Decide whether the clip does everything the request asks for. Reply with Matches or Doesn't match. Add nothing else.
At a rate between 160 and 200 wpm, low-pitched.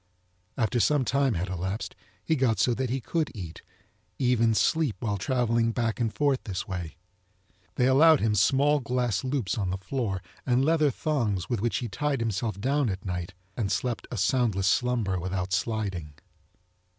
Matches